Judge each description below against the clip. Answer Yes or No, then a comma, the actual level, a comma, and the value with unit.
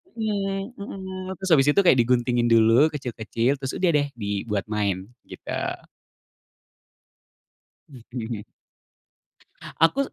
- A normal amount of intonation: No, wide, 8.6 semitones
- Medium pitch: No, low, 130 Hz